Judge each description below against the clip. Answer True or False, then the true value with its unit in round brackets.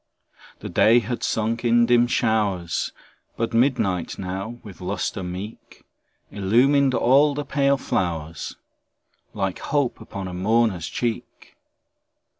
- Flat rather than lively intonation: False (4.3 semitones)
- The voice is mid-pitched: False (110 Hz)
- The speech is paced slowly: True (115 wpm)